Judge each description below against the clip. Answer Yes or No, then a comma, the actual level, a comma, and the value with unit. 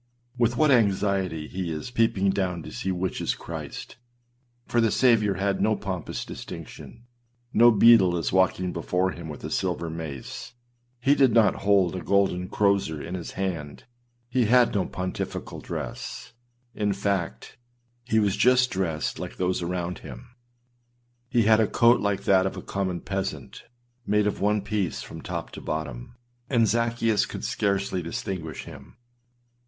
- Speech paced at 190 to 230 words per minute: No, average, 160 wpm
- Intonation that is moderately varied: Yes, average, 3.8 semitones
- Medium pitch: No, low, 100 Hz